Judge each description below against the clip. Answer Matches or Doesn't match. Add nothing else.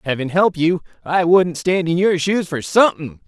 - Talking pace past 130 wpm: Matches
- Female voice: Doesn't match